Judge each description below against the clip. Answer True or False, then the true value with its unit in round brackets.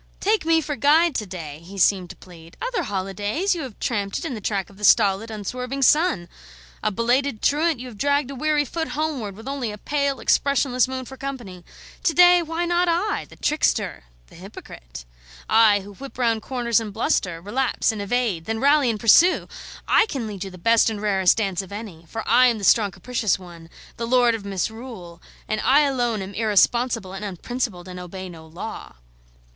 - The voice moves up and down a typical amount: False (5.9 semitones)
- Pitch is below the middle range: False (225 Hz)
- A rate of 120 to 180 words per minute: False (200 wpm)